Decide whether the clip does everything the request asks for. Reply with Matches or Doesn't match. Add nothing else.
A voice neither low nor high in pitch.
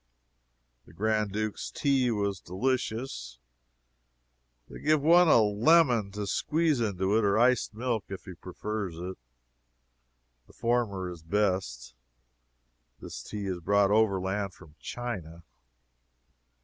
Doesn't match